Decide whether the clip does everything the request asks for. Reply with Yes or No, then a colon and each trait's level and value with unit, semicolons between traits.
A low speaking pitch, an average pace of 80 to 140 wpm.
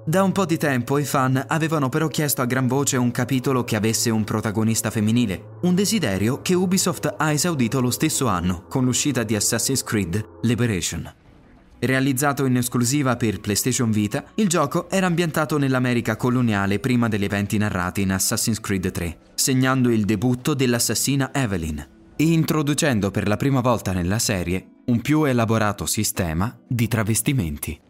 No: low, 120 Hz; average, 160 wpm